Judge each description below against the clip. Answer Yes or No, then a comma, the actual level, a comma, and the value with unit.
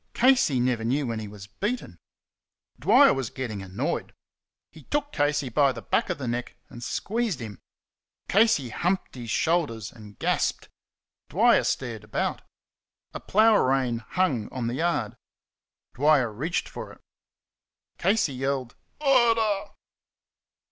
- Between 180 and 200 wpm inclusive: No, slow, 135 wpm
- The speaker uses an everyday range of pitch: No, wide, 7.9 semitones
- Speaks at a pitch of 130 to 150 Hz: Yes, low, 135 Hz